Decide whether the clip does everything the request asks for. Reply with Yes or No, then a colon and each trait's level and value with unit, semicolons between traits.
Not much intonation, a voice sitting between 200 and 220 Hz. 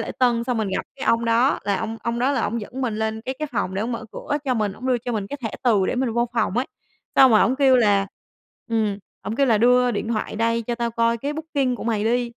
No: narrow, 2.3 semitones; high, 235 Hz